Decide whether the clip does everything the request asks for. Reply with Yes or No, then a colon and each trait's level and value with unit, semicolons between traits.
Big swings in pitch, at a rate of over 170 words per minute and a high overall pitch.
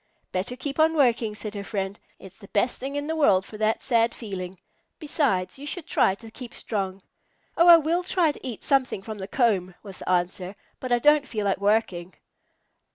Yes: wide, 6.5 semitones; fast, 205 wpm; high, 220 Hz